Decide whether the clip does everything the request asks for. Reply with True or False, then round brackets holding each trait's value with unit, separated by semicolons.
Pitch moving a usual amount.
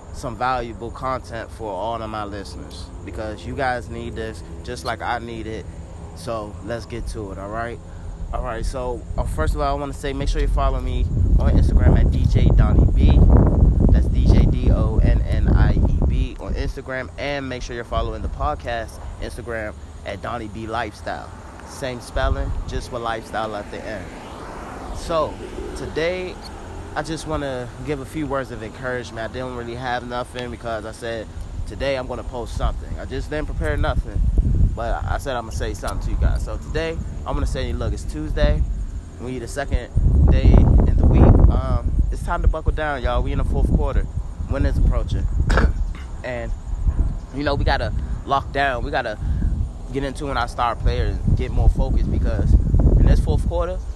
False (6.4 semitones)